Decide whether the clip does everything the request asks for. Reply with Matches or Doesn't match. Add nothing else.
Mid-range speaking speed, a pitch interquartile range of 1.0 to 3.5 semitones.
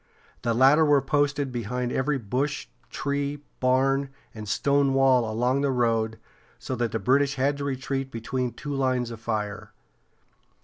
Matches